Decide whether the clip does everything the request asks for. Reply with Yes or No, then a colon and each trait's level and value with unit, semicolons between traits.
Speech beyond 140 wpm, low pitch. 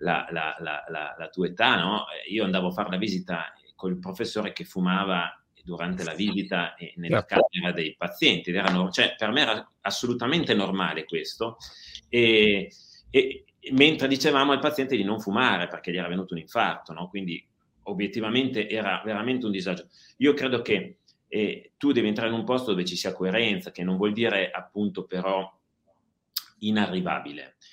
Yes: average, 165 wpm; low, 100 Hz